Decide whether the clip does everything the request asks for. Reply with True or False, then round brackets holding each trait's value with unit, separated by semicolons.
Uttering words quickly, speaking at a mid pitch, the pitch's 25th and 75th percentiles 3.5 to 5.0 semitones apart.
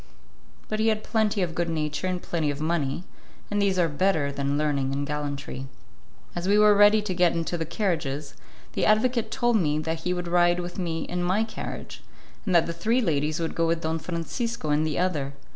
True (210 wpm; 170 Hz; 4.4 semitones)